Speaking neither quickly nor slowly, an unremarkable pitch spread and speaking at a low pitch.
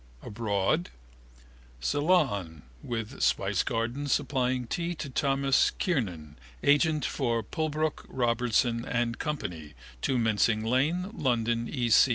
No: slow, 100 wpm; average, 4.6 semitones; low, 120 Hz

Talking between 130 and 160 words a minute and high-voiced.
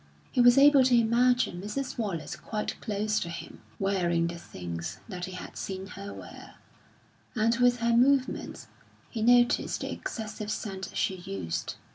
Yes: average, 155 wpm; high, 215 Hz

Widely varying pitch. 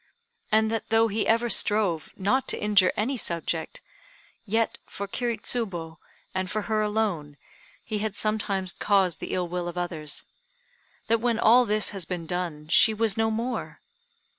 No: average, 3.9 semitones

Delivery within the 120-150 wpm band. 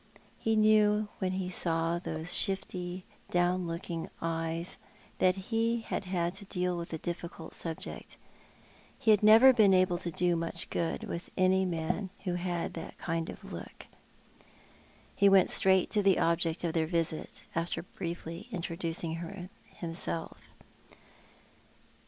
Yes: slow, 135 wpm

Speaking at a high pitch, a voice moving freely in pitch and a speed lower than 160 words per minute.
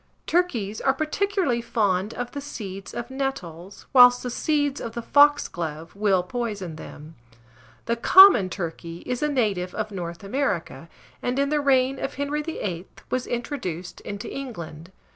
Yes: high, 235 Hz; wide, 7.1 semitones; average, 150 wpm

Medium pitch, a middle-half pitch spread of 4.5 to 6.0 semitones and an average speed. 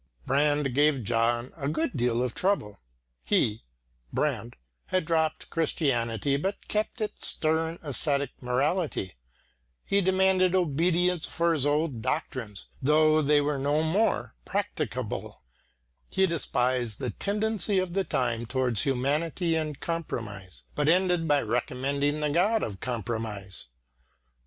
No: medium, 145 Hz; wide, 5.4 semitones; slow, 125 wpm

